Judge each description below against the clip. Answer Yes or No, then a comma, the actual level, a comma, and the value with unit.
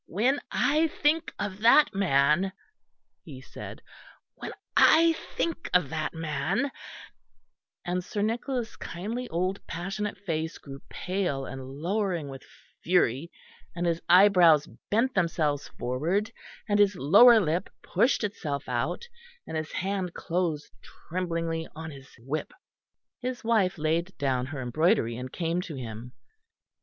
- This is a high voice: No, medium, 175 Hz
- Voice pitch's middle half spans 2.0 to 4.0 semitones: No, wide, 5.5 semitones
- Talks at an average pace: No, slow, 130 wpm